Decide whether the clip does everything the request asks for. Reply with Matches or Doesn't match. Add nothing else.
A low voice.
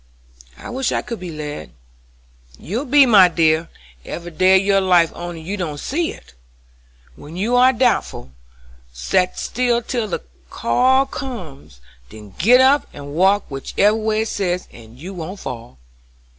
Doesn't match